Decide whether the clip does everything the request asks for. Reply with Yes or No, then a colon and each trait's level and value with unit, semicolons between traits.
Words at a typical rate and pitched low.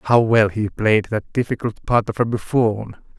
Yes: average, 170 wpm; low, 110 Hz